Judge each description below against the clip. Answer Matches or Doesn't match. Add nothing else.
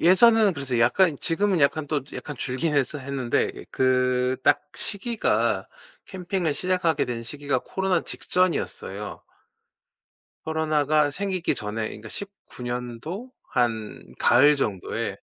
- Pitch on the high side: Doesn't match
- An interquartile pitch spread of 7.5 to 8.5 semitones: Doesn't match